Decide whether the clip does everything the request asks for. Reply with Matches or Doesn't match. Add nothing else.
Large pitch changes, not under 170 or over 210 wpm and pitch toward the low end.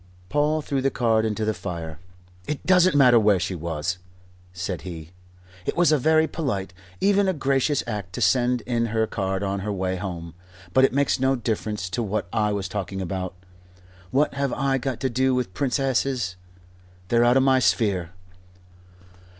Matches